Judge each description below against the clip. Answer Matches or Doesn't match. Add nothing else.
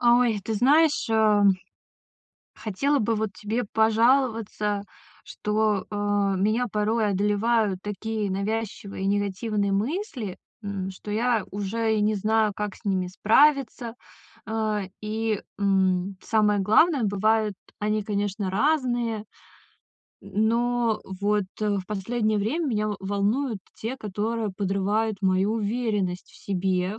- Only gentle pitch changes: Matches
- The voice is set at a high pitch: Matches